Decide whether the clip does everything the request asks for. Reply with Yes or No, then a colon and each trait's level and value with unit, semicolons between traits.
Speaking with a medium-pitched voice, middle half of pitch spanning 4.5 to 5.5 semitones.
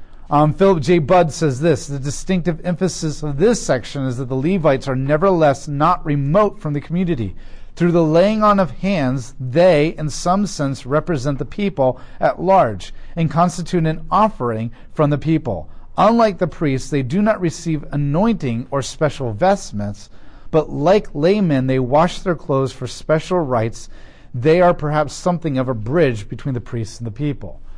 Yes: medium, 150 Hz; average, 5.2 semitones